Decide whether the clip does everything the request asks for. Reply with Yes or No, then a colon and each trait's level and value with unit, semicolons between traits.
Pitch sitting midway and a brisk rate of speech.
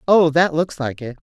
Yes: medium, 155 Hz; fast, 235 wpm